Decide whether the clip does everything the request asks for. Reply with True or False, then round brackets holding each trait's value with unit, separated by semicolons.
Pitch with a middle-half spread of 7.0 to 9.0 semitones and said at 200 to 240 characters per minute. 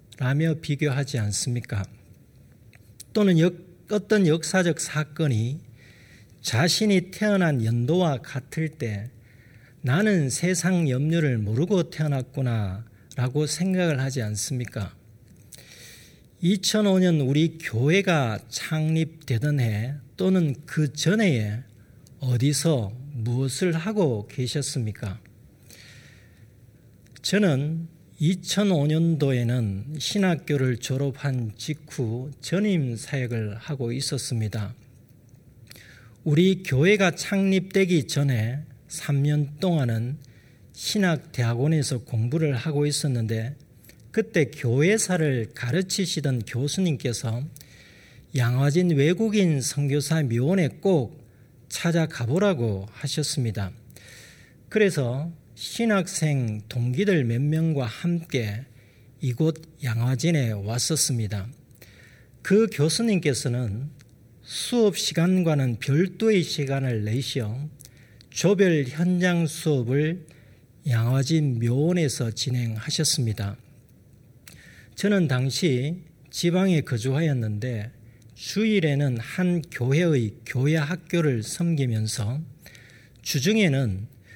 False (5.4 semitones; 205 characters per minute)